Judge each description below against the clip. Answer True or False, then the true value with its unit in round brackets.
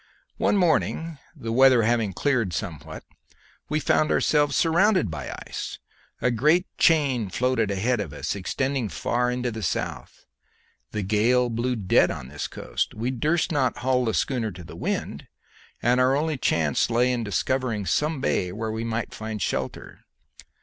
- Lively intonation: False (4.2 semitones)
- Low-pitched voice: True (120 Hz)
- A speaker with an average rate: True (165 wpm)